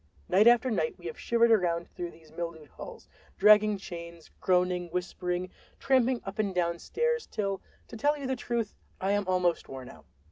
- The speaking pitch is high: Yes, high, 195 Hz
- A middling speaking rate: Yes, average, 180 wpm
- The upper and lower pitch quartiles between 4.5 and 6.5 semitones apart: Yes, average, 5.0 semitones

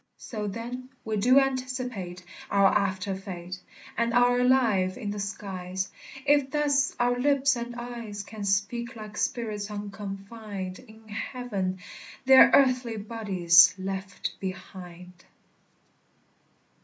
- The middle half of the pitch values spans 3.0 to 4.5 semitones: Yes, average, 4.2 semitones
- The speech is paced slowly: Yes, slow, 115 wpm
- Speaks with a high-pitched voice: Yes, high, 210 Hz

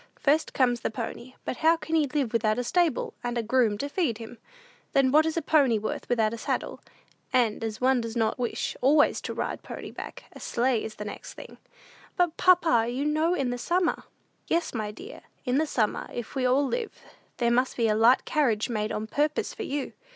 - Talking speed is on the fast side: Yes, fast, 215 wpm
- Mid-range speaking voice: No, very high, 250 Hz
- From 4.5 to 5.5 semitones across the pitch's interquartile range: Yes, average, 4.8 semitones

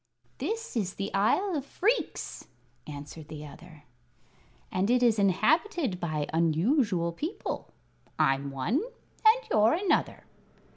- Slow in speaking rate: Yes, slow, 115 wpm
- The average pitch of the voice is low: No, high, 200 Hz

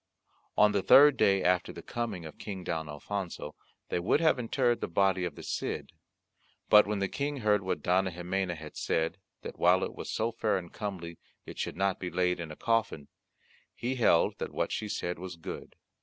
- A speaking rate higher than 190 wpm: Yes, average, 200 wpm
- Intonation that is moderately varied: Yes, average, 3.5 semitones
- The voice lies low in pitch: Yes, very low, 95 Hz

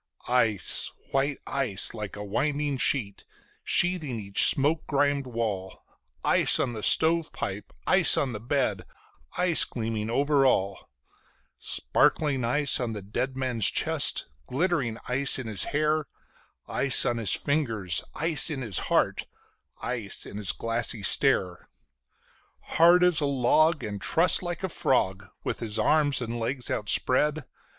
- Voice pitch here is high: No, low, 130 Hz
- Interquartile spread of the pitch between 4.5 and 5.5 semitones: Yes, average, 5.2 semitones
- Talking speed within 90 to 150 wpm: Yes, average, 140 wpm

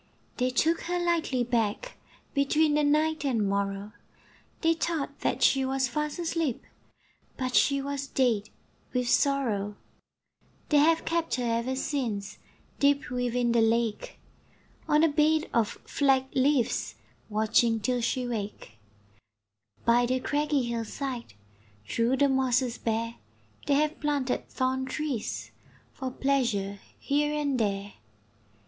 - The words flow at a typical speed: No, slow, 130 wpm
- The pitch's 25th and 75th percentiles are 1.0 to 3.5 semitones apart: No, average, 4.0 semitones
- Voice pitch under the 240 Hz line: No, very high, 260 Hz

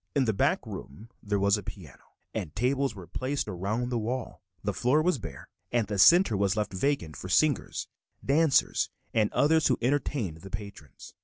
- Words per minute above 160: Yes, average, 180 wpm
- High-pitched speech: No, low, 110 Hz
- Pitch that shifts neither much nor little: No, wide, 5.7 semitones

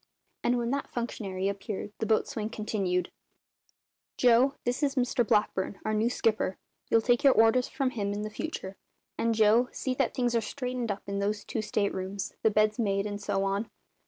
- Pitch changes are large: No, average, 3.2 semitones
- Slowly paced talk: No, average, 185 wpm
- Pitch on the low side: No, high, 215 Hz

